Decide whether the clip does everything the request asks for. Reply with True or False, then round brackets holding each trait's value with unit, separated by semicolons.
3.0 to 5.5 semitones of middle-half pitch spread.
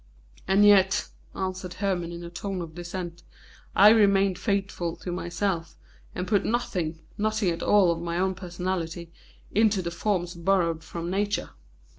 False (2.6 semitones)